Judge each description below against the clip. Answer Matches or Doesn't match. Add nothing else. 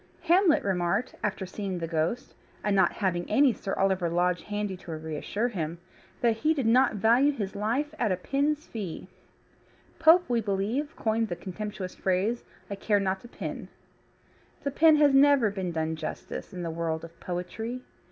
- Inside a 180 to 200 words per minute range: Doesn't match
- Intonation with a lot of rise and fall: Matches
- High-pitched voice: Matches